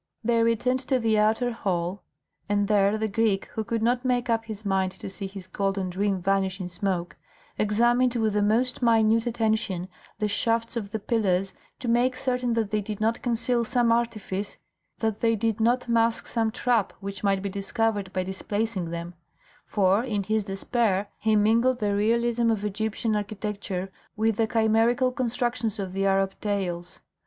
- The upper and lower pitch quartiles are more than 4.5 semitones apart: No, average, 2.9 semitones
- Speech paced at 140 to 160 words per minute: No, average, 175 wpm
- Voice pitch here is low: No, high, 215 Hz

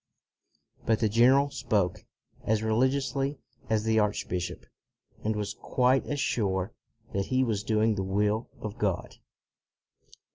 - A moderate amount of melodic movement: Yes, average, 3.5 semitones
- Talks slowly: Yes, slow, 130 wpm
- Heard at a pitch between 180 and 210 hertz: No, low, 110 Hz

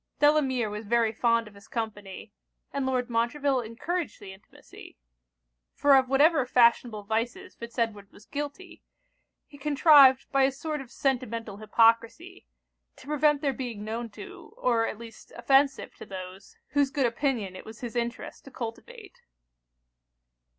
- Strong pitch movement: No, average, 4.0 semitones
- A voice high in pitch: Yes, high, 245 Hz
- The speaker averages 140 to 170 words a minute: Yes, average, 150 wpm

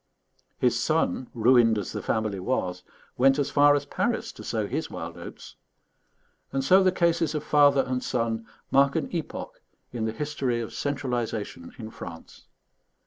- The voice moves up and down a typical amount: Yes, average, 4.3 semitones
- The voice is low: Yes, low, 130 Hz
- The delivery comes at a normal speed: Yes, average, 160 wpm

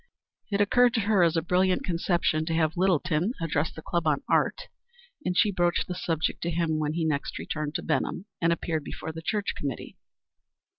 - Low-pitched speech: No, medium, 170 Hz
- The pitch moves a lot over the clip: No, narrow, 2.6 semitones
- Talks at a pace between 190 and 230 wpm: Yes, average, 195 wpm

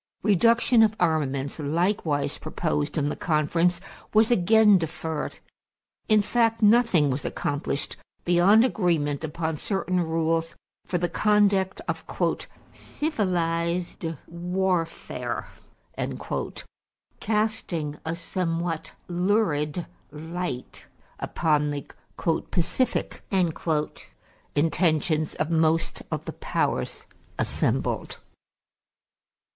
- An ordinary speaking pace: No, slow, 85 wpm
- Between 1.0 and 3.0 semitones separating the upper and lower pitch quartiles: No, average, 3.8 semitones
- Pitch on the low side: No, medium, 170 Hz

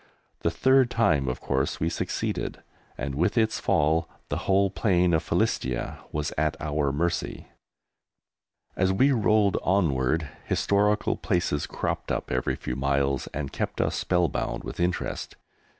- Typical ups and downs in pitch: No, wide, 5.7 semitones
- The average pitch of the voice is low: Yes, very low, 85 Hz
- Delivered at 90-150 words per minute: Yes, average, 140 wpm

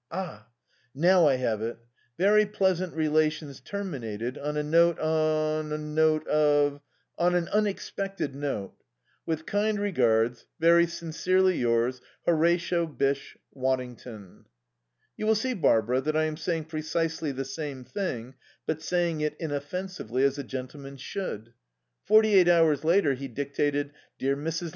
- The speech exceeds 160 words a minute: No, average, 140 wpm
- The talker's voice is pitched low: No, medium, 155 Hz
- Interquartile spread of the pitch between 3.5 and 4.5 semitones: Yes, average, 4.1 semitones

